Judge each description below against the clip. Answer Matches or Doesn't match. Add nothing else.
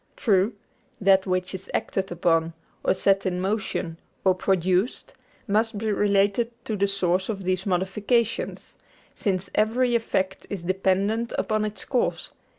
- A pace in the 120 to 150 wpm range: Matches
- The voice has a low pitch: Doesn't match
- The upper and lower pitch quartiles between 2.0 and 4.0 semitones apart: Matches